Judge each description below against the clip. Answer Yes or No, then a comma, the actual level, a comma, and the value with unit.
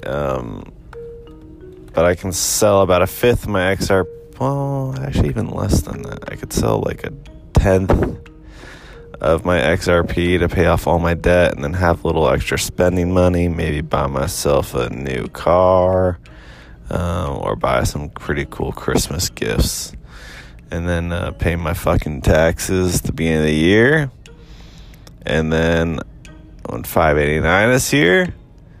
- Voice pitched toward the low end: Yes, very low, 90 Hz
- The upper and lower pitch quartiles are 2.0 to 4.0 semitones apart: Yes, average, 2.9 semitones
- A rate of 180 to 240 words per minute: No, average, 150 wpm